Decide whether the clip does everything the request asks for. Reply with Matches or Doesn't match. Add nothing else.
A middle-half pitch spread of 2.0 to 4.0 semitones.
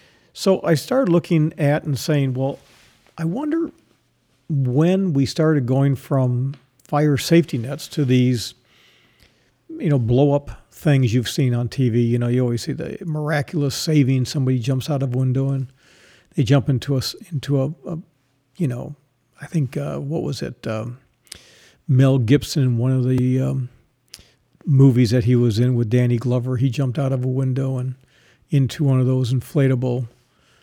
Matches